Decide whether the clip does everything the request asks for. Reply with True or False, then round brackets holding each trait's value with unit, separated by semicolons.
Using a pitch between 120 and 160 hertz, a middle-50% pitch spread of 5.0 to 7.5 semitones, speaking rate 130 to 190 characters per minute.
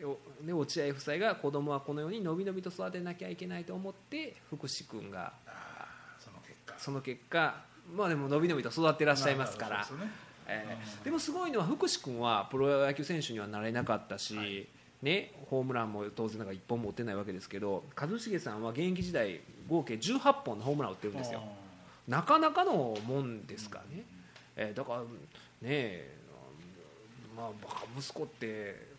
False (140 Hz; 7.0 semitones; 330 characters per minute)